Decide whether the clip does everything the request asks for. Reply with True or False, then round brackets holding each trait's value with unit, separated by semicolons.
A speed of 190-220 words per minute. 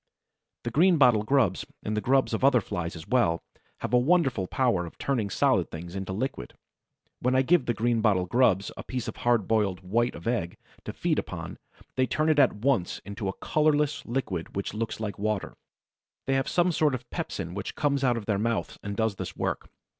True (200 wpm)